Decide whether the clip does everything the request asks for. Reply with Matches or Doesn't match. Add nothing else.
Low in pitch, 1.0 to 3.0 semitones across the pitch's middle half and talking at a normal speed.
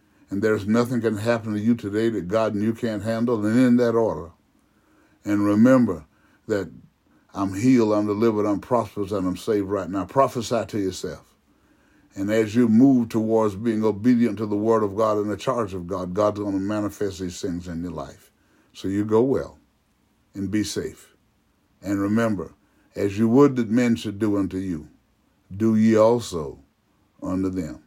Matches